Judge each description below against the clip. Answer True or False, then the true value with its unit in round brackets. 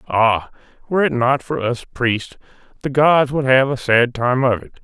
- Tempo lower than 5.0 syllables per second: True (4.5 syllables/s)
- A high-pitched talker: False (130 Hz)